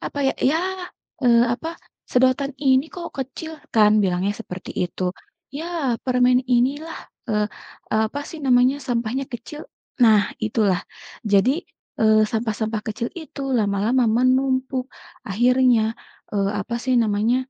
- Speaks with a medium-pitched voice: No, high, 245 Hz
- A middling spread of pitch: Yes, average, 3.7 semitones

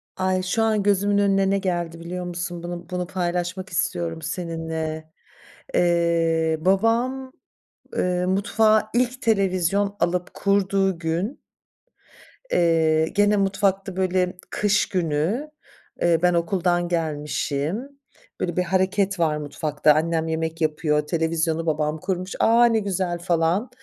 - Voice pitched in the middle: Yes, medium, 180 Hz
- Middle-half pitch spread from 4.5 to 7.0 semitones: No, average, 3.2 semitones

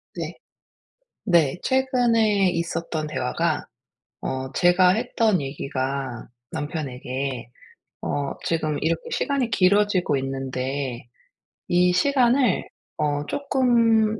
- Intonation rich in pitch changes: Yes, wide, 8.3 semitones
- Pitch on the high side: No, medium, 170 Hz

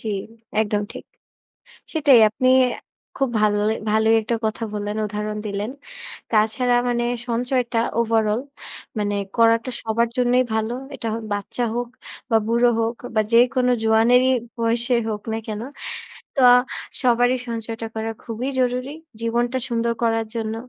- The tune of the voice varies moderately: No, narrow, 1.8 semitones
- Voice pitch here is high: Yes, high, 230 Hz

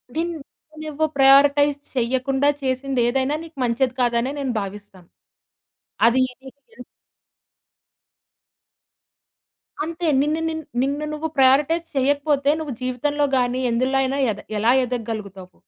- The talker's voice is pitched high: Yes, very high, 270 Hz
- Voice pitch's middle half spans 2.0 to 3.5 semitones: Yes, average, 2.9 semitones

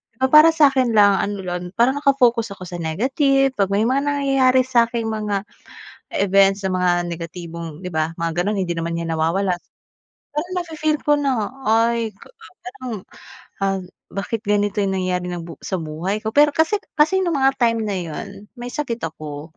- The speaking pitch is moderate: No, high, 210 Hz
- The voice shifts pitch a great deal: Yes, wide, 6.5 semitones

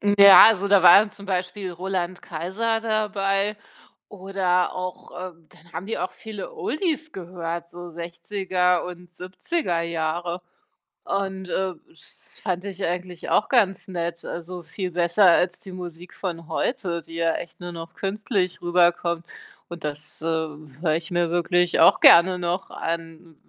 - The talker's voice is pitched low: No, medium, 180 Hz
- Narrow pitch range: Yes, narrow, 2.3 semitones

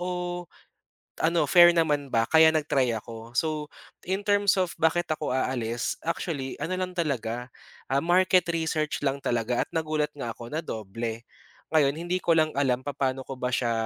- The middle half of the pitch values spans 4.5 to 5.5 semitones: Yes, average, 5.1 semitones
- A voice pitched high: No, medium, 150 Hz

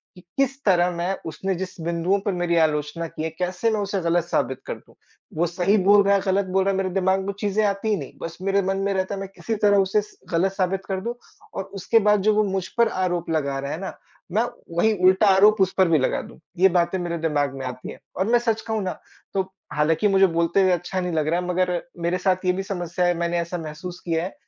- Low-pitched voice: No, medium, 185 Hz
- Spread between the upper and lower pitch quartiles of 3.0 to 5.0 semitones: No, narrow, 2.6 semitones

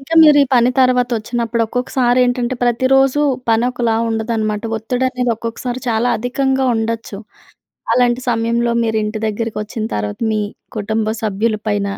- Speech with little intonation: Yes, narrow, 2.1 semitones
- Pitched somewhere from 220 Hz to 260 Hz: Yes, high, 235 Hz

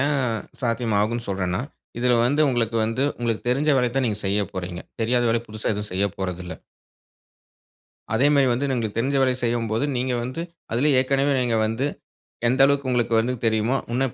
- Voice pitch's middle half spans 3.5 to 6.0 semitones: No, average, 3.1 semitones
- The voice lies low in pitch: Yes, low, 120 Hz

